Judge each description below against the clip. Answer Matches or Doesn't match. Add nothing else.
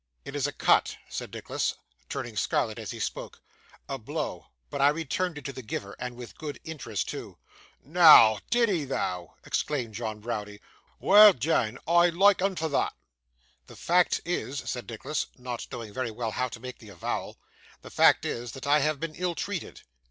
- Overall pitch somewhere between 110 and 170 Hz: Matches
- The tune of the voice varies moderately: Doesn't match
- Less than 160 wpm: Doesn't match